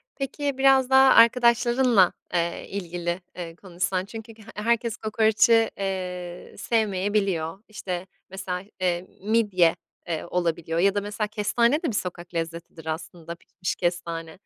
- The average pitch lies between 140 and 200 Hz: Yes, high, 190 Hz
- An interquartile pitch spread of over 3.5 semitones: Yes, average, 4.4 semitones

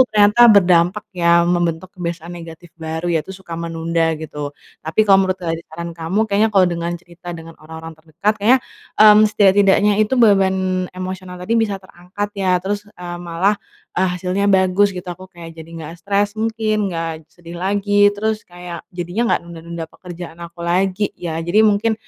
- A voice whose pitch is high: No, medium, 180 Hz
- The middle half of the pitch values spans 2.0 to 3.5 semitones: Yes, average, 3.2 semitones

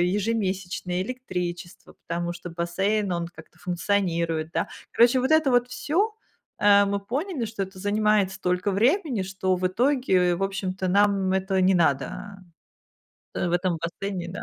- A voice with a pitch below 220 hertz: Yes, high, 190 Hz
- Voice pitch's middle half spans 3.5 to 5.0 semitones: No, average, 3.1 semitones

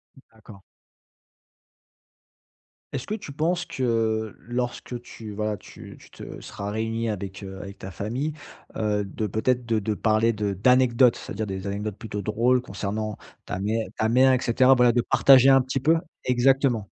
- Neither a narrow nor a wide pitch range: Yes, average, 3.3 semitones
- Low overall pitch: Yes, low, 115 Hz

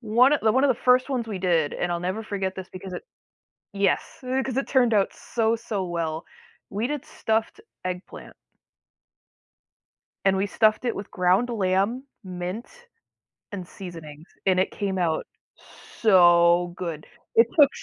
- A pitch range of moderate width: Yes, average, 4.4 semitones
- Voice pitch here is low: No, high, 195 Hz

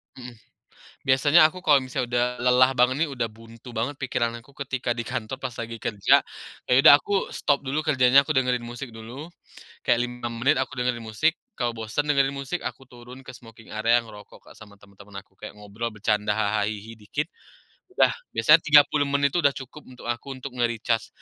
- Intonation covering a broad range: No, average, 3.3 semitones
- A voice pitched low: Yes, low, 125 Hz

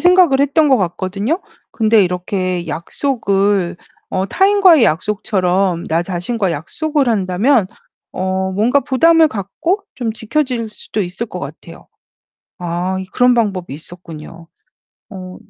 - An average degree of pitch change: No, wide, 6.4 semitones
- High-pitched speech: Yes, high, 200 Hz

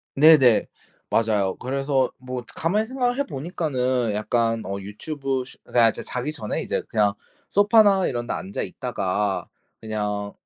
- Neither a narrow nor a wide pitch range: No, wide, 6.3 semitones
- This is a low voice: Yes, low, 125 Hz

